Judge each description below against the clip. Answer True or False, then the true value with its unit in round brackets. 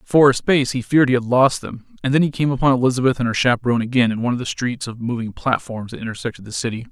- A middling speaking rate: False (270 wpm)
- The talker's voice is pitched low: True (125 Hz)